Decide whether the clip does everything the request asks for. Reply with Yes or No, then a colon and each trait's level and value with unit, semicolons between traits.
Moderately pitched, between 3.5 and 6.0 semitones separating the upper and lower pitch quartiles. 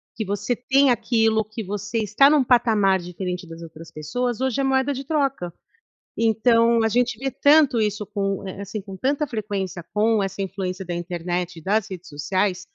No: high, 210 Hz; average, 4.6 semitones